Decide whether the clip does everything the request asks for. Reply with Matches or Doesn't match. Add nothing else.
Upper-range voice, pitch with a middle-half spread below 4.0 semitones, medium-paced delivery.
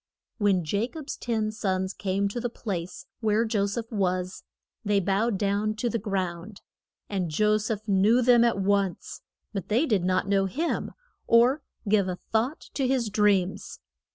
Matches